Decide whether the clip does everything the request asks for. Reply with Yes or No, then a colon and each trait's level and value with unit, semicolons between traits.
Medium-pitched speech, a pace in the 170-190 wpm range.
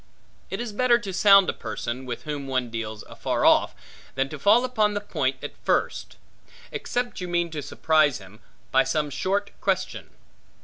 Yes: medium, 170 Hz; average, 175 wpm